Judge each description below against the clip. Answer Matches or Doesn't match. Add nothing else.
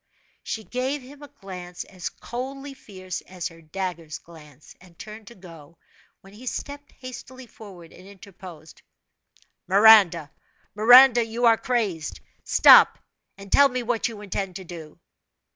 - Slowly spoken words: Doesn't match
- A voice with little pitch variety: Doesn't match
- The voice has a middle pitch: Doesn't match